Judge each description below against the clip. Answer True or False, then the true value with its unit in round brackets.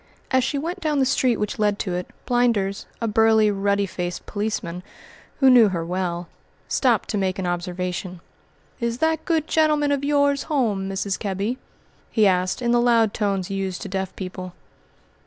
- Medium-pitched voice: False (210 Hz)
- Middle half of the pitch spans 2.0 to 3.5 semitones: False (5.1 semitones)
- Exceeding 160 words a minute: True (175 wpm)